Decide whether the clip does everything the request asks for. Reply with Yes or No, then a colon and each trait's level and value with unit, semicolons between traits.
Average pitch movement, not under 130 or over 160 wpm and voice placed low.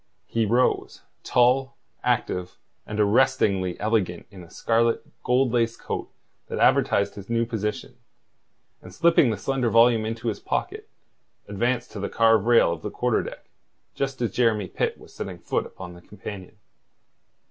Yes: average, 3.2 semitones; average, 155 wpm; low, 115 Hz